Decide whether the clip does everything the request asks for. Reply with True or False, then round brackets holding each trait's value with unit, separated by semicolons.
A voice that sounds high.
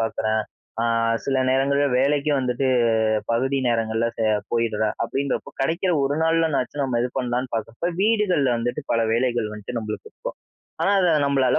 False (130 Hz)